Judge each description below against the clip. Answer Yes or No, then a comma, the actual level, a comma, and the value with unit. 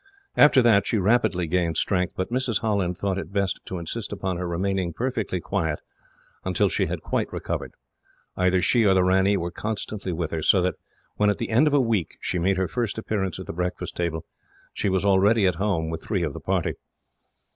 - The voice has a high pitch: No, very low, 95 Hz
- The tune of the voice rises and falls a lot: No, average, 2.9 semitones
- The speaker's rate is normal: No, fast, 210 wpm